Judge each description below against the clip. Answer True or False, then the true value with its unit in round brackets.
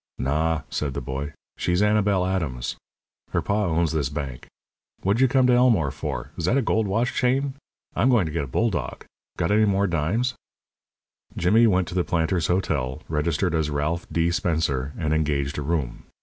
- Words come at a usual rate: True (180 wpm)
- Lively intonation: True (5.7 semitones)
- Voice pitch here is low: True (85 Hz)